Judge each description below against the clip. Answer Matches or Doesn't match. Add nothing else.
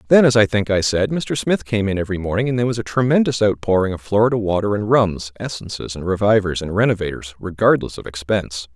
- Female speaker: Doesn't match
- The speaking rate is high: Matches